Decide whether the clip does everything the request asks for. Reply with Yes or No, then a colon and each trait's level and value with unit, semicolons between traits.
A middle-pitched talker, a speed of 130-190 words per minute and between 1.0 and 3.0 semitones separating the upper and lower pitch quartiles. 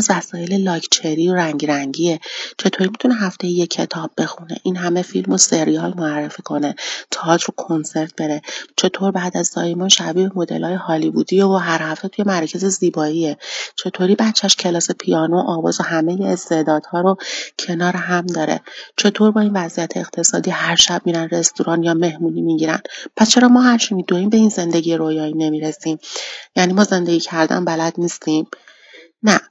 Yes: medium, 175 Hz; fast, 155 wpm; average, 2.7 semitones